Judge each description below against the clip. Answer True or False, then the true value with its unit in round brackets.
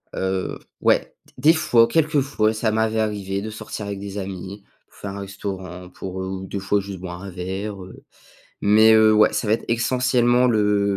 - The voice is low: True (100 Hz)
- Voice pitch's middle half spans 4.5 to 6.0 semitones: False (2.6 semitones)